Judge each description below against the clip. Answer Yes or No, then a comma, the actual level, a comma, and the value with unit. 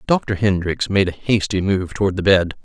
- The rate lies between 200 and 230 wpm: Yes, fast, 205 wpm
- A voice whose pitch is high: No, very low, 95 Hz